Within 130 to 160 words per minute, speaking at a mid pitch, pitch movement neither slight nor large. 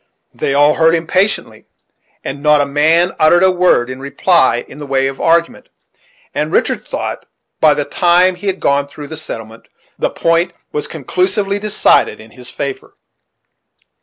No: average, 170 wpm; medium, 155 Hz; average, 4.4 semitones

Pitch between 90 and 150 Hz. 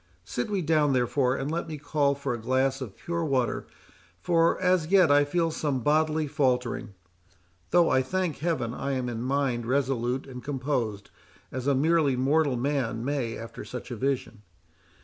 Yes: low, 135 Hz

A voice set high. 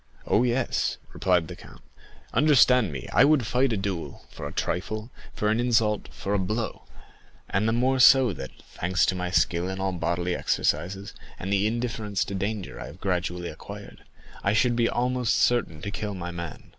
No: low, 100 Hz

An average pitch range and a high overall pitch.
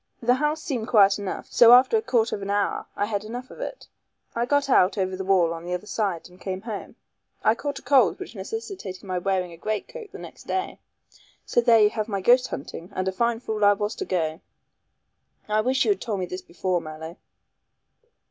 Yes: average, 4.6 semitones; high, 210 Hz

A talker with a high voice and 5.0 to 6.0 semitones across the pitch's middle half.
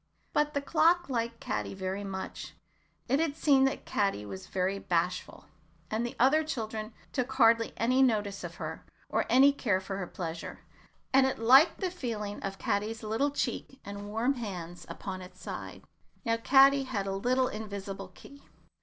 Yes: high, 225 Hz; average, 5.3 semitones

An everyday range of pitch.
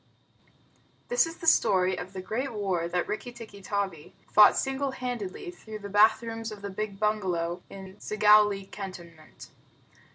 Yes: average, 3.0 semitones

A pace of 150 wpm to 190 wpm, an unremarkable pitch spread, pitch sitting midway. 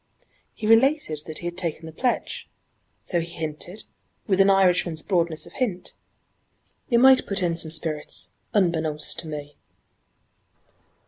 No: average, 140 wpm; average, 3.9 semitones; medium, 170 Hz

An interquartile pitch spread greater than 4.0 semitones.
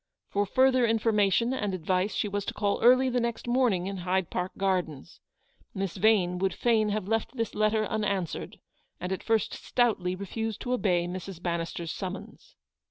No: average, 3.5 semitones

